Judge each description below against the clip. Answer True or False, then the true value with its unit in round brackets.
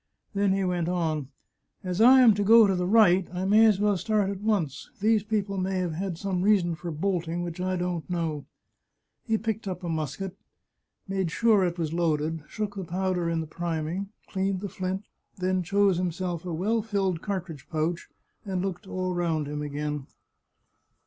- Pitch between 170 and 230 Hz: True (185 Hz)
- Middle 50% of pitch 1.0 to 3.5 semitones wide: True (2.9 semitones)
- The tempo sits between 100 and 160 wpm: False (190 wpm)